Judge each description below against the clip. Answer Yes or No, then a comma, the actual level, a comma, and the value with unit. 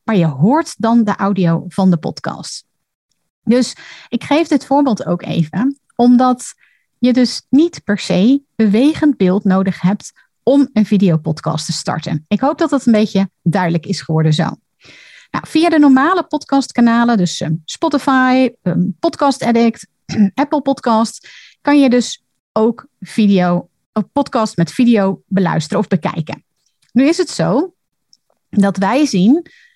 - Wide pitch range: Yes, wide, 6.6 semitones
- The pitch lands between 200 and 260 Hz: Yes, high, 225 Hz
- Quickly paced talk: No, average, 140 wpm